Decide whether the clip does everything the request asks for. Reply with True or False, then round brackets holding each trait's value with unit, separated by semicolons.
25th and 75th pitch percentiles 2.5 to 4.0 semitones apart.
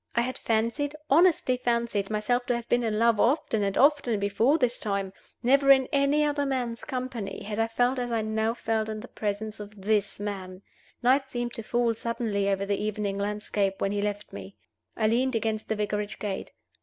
True (3.2 semitones)